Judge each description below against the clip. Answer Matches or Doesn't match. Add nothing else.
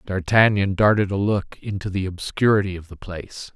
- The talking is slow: Doesn't match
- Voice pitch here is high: Doesn't match